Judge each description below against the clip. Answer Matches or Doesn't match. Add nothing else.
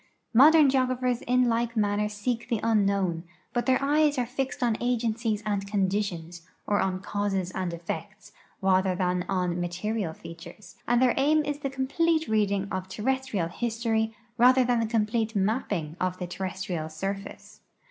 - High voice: Matches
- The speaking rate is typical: Matches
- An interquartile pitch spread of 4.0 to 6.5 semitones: Matches